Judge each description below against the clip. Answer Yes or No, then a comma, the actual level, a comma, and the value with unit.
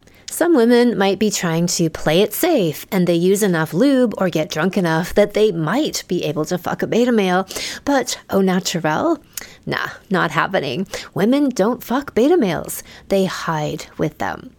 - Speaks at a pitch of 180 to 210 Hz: Yes, high, 190 Hz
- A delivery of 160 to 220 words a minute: Yes, average, 175 wpm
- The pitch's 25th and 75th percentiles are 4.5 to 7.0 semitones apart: Yes, average, 5.3 semitones